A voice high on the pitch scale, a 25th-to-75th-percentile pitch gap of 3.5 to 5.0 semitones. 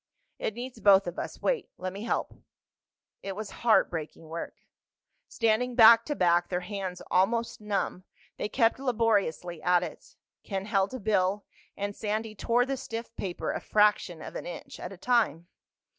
Yes: high, 205 Hz; average, 4.0 semitones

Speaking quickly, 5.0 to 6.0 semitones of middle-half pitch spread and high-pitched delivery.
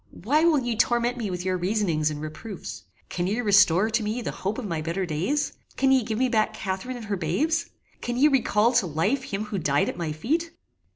Yes: fast, 225 wpm; wide, 5.6 semitones; high, 215 Hz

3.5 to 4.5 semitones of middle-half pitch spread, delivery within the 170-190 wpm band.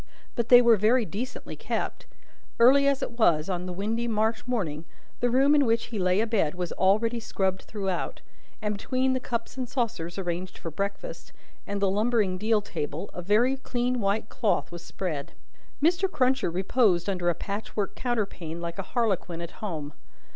No: average, 4.9 semitones; average, 175 wpm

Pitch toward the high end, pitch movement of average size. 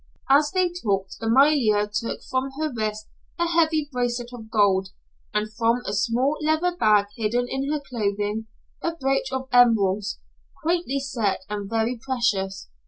Yes: high, 240 Hz; average, 4.7 semitones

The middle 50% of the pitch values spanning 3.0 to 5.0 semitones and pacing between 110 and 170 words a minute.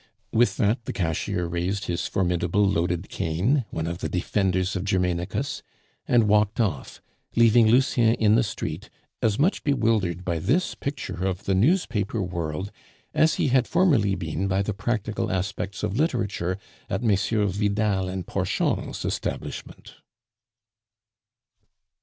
Yes: average, 4.0 semitones; slow, 135 wpm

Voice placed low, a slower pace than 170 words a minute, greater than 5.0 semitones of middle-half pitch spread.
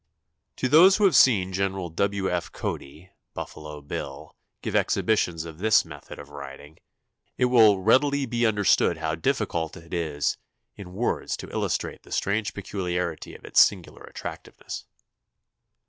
Yes: very low, 90 Hz; average, 145 wpm; wide, 5.5 semitones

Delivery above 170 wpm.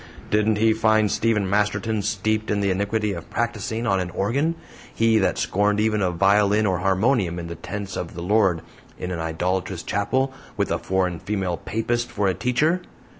Yes: average, 180 wpm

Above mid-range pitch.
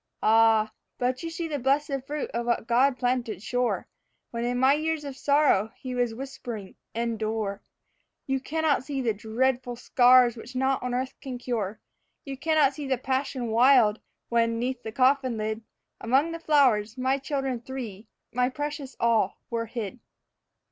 Yes: very high, 250 Hz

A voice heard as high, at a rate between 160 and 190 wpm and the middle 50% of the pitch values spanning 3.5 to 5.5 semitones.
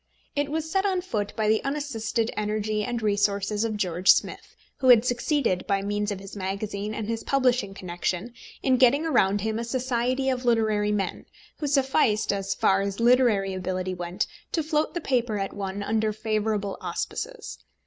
Yes: high, 215 Hz; average, 175 wpm; average, 4.0 semitones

